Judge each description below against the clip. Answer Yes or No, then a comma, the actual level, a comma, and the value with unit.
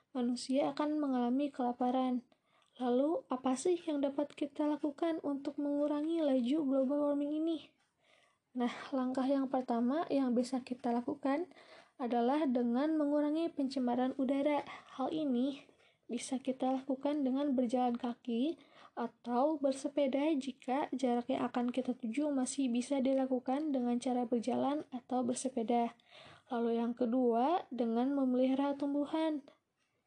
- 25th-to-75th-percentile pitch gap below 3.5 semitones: Yes, average, 2.8 semitones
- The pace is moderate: Yes, average, 120 wpm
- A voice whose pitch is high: Yes, very high, 265 Hz